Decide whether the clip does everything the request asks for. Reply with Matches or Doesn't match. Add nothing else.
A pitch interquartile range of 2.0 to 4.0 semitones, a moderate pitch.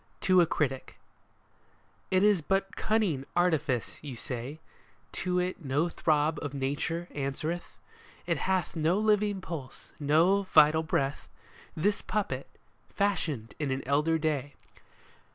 Doesn't match